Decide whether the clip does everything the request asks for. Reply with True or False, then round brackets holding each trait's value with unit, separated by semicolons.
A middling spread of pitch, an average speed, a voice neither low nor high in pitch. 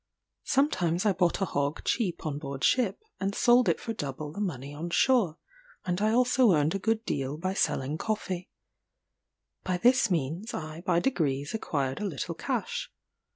False (6.6 semitones; 170 wpm; 175 Hz)